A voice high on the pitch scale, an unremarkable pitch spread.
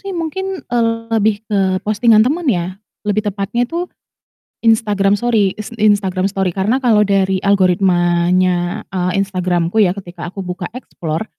Yes: high, 200 Hz; average, 3.3 semitones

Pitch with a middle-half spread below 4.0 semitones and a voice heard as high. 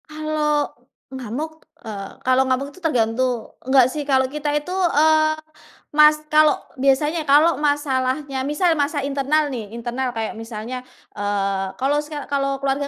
Yes: average, 2.9 semitones; very high, 280 Hz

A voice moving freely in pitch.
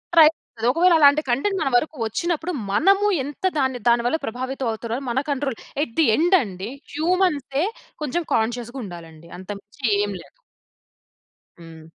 Yes: wide, 6.1 semitones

